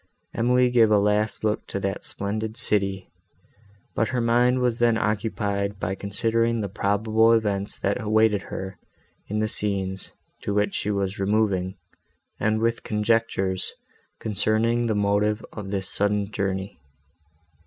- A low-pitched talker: Yes, low, 105 Hz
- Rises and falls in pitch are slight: Yes, narrow, 2.1 semitones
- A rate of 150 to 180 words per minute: No, average, 140 wpm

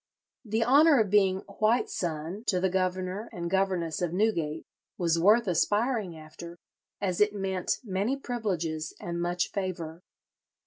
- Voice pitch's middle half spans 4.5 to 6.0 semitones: No, average, 3.5 semitones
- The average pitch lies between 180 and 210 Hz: Yes, medium, 185 Hz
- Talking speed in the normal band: Yes, average, 145 wpm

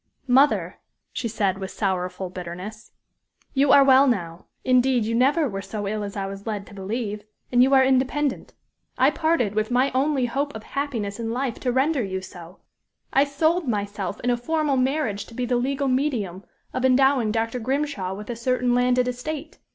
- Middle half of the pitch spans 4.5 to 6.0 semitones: Yes, average, 4.8 semitones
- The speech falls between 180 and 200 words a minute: Yes, average, 185 wpm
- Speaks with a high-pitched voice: Yes, high, 245 Hz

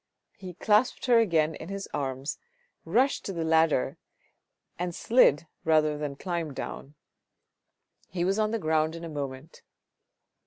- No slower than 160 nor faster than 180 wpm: No, average, 150 wpm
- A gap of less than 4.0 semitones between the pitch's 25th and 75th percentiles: No, average, 4.3 semitones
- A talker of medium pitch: Yes, medium, 165 Hz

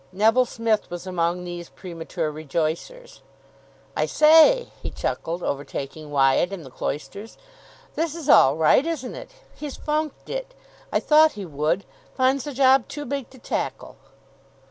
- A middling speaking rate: Yes, average, 145 wpm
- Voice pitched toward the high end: Yes, high, 210 Hz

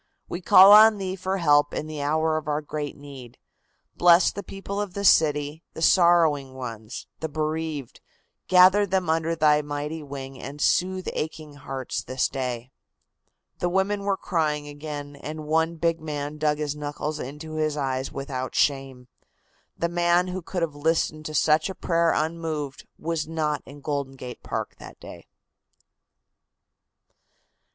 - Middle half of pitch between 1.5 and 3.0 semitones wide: Yes, average, 2.7 semitones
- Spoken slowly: No, average, 155 wpm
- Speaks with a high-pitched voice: No, medium, 155 Hz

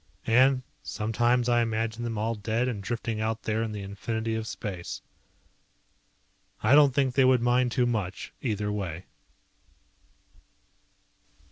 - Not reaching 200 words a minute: Yes, slow, 135 wpm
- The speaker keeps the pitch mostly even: Yes, narrow, 2.3 semitones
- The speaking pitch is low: Yes, low, 115 Hz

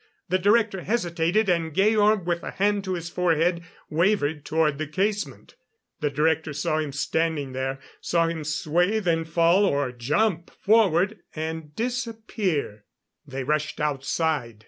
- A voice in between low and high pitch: Yes, medium, 165 Hz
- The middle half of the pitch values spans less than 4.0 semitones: No, average, 4.5 semitones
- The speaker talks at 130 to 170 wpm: Yes, average, 140 wpm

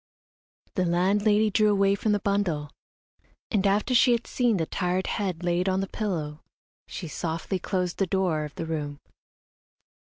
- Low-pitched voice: No, high, 190 Hz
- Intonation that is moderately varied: Yes, average, 3.4 semitones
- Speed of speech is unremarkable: Yes, average, 160 wpm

